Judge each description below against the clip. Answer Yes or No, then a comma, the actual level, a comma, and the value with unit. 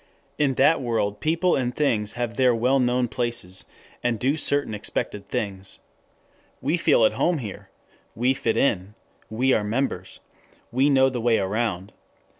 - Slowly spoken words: No, average, 155 wpm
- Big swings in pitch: No, average, 4.1 semitones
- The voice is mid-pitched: No, low, 120 Hz